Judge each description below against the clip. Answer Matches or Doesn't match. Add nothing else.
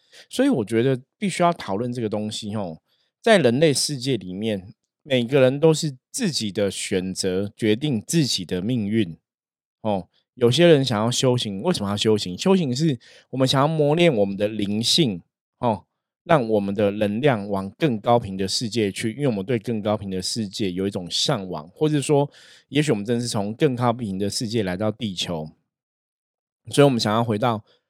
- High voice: Doesn't match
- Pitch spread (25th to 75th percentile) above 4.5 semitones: Matches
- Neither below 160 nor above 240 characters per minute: Doesn't match